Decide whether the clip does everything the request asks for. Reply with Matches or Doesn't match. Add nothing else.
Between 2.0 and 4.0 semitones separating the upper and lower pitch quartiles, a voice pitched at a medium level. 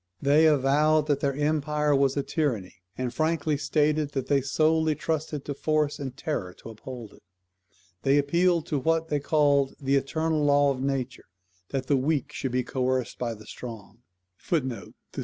Matches